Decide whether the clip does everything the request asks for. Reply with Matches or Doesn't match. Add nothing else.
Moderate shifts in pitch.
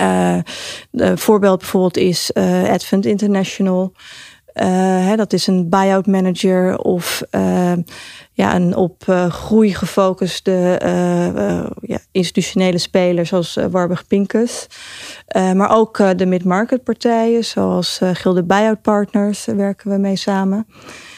Doesn't match